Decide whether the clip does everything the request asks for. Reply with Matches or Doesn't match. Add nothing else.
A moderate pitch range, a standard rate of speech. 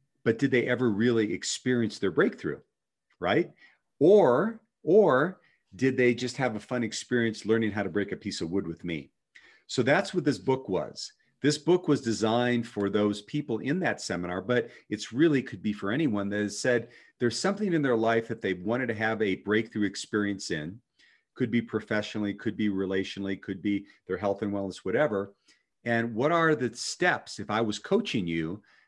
Matches